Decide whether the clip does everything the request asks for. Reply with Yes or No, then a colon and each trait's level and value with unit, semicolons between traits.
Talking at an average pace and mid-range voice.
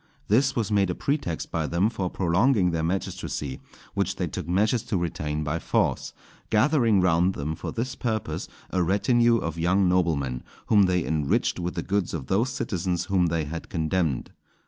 No: average, 175 wpm; very low, 90 Hz